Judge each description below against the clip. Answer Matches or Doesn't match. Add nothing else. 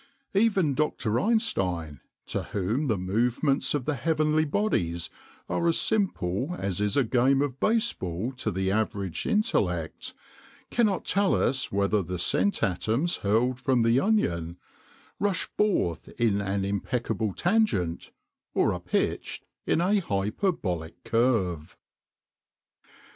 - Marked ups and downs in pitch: Matches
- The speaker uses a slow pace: Matches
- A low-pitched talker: Matches